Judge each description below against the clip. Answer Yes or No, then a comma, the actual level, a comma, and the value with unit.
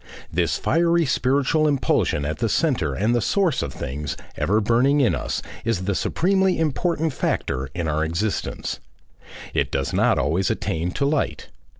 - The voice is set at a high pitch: No, low, 115 Hz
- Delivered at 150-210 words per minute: Yes, average, 160 wpm